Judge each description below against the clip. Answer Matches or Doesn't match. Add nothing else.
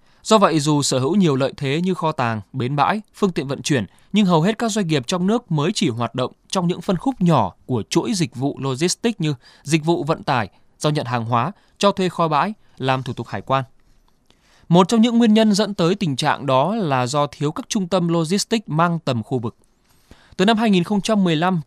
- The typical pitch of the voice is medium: Matches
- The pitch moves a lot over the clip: Matches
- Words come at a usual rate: Matches